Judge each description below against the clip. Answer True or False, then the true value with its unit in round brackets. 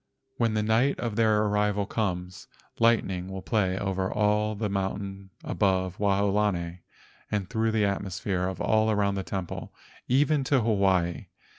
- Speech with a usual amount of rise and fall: False (2.3 semitones)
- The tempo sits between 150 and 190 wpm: False (140 wpm)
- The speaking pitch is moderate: False (100 Hz)